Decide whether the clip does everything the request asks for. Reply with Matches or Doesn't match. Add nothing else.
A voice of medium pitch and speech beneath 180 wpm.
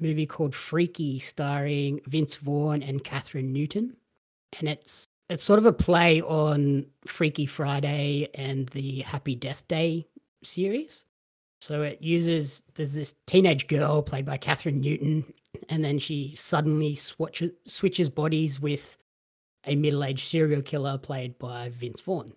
Matches